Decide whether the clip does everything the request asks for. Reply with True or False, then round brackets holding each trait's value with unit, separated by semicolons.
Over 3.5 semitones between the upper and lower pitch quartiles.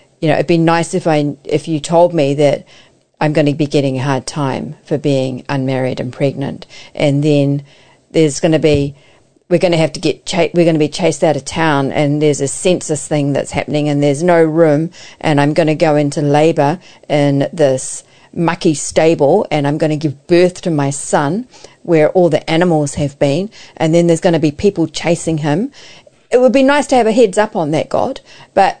False (2.9 semitones)